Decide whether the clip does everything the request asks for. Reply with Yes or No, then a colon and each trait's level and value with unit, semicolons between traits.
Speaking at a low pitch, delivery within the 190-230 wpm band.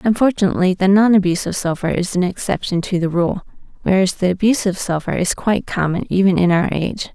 No: medium, 185 Hz; average, 200 wpm